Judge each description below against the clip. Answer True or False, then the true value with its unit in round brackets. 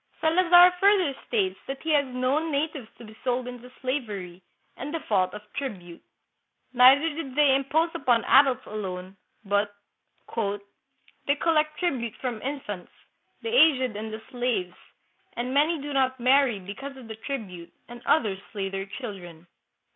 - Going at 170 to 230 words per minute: False (150 wpm)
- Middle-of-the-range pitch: False (250 Hz)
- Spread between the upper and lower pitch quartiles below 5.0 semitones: False (5.6 semitones)